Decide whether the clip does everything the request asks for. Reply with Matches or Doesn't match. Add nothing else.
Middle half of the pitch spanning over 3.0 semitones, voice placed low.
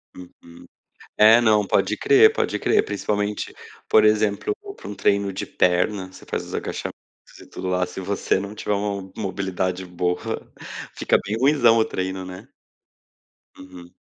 Doesn't match